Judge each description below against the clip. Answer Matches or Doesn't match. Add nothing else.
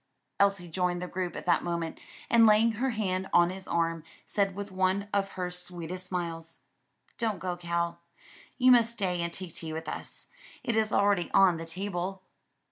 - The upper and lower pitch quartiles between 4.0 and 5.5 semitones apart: Doesn't match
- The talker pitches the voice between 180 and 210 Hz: Matches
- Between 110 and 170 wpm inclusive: Doesn't match